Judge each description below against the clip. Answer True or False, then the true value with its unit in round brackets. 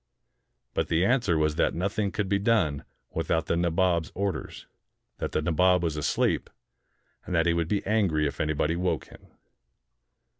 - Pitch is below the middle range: True (85 Hz)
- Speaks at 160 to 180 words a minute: True (165 wpm)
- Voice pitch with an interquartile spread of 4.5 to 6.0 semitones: False (3.6 semitones)